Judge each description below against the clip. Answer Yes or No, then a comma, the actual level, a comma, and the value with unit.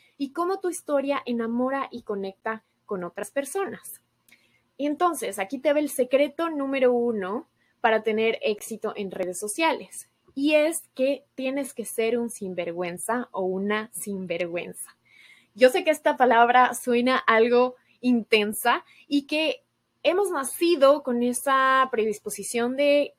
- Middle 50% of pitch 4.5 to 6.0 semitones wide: Yes, average, 4.8 semitones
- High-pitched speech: Yes, very high, 250 Hz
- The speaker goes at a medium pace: Yes, average, 135 wpm